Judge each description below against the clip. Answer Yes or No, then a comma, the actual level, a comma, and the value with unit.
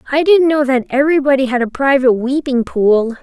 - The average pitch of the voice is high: Yes, very high, 270 Hz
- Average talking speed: Yes, average, 185 wpm